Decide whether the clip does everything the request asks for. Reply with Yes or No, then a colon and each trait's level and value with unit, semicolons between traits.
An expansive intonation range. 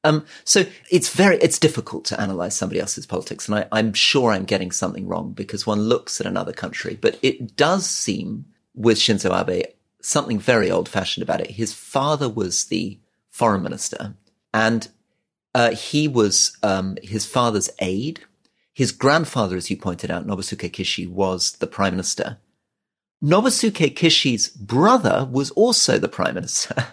Yes: wide, 7.8 semitones